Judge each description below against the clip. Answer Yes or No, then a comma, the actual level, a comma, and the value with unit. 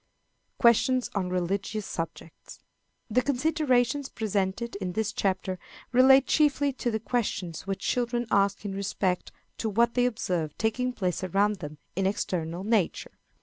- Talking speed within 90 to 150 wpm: Yes, average, 140 wpm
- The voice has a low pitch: No, high, 210 Hz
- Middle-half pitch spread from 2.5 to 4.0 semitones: No, average, 4.7 semitones